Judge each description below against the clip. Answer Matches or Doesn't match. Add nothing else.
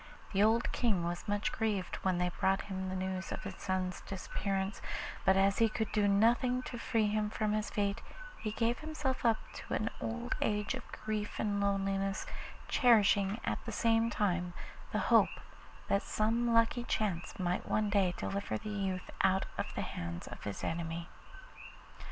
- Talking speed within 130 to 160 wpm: Doesn't match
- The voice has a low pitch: Doesn't match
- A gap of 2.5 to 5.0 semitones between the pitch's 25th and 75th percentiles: Matches